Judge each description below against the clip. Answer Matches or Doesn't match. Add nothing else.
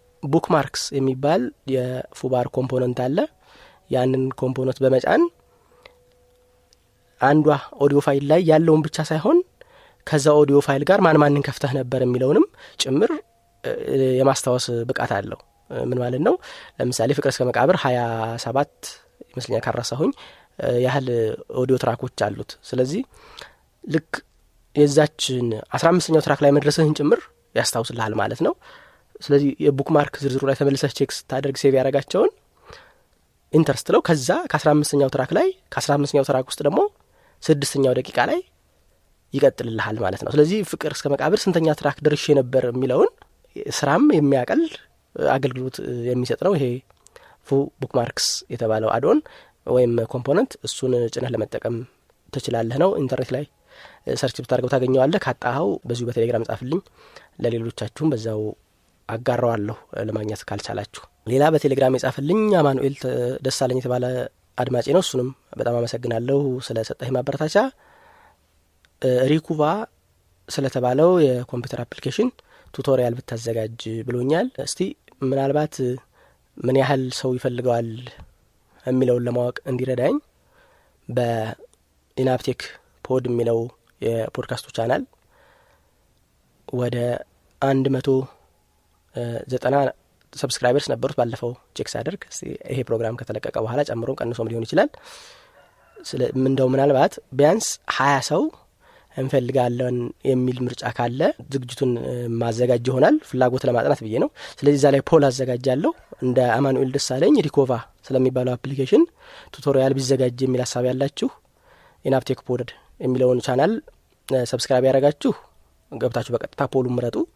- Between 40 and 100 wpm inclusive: Doesn't match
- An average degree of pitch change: Matches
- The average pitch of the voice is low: Matches